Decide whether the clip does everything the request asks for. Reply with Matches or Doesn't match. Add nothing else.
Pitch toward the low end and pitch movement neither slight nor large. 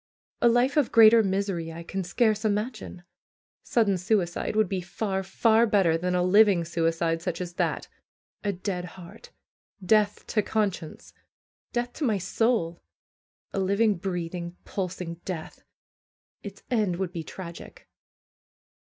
Doesn't match